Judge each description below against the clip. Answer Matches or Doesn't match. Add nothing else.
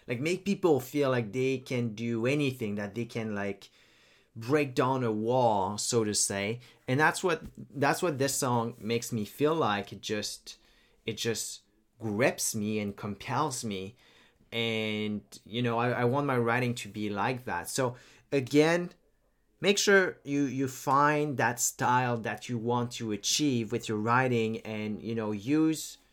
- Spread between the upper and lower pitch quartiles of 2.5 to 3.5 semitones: Doesn't match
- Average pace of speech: Matches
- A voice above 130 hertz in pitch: Doesn't match